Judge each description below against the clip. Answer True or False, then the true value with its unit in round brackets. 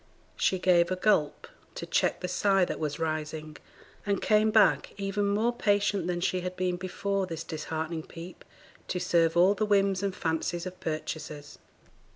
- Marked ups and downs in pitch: False (3.4 semitones)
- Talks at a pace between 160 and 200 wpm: True (170 wpm)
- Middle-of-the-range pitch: True (180 Hz)